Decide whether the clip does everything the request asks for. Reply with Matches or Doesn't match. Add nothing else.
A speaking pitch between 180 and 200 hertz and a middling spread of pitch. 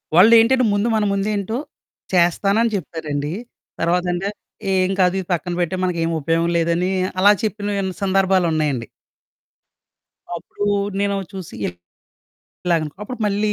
Matches